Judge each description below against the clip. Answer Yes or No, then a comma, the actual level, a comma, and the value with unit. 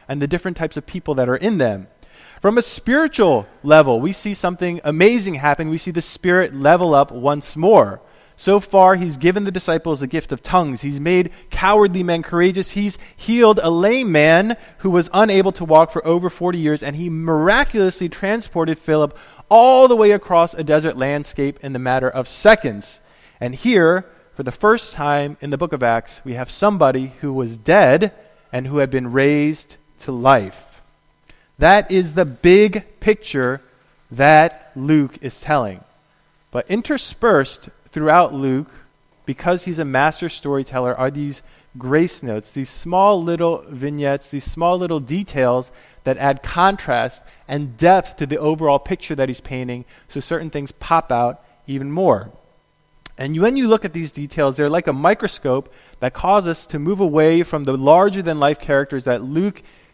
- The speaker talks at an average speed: Yes, average, 170 wpm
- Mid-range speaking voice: Yes, medium, 160 Hz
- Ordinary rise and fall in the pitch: Yes, average, 5.0 semitones